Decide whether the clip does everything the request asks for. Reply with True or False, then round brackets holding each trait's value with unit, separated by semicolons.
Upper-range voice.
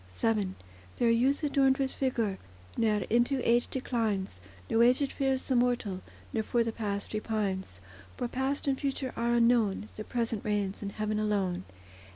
True (230 Hz)